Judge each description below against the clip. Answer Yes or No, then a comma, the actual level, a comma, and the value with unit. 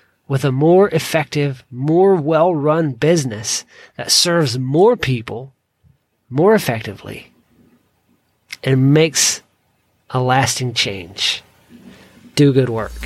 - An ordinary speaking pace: No, slow, 100 wpm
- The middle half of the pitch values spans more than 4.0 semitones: Yes, average, 4.5 semitones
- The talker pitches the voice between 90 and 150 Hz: Yes, medium, 140 Hz